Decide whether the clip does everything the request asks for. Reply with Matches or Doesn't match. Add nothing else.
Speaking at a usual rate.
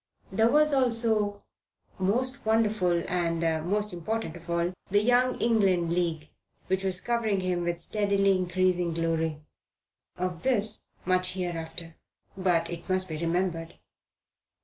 Doesn't match